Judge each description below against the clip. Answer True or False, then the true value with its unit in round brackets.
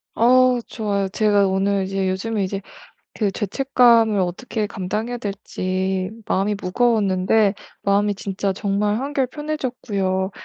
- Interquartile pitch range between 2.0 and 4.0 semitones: True (3.3 semitones)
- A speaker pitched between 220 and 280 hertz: False (205 Hz)